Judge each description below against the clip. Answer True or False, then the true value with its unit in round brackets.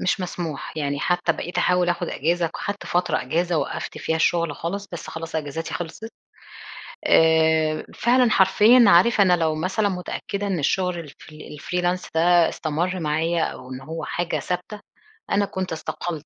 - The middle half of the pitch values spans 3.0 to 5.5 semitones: False (2.4 semitones)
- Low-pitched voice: False (175 Hz)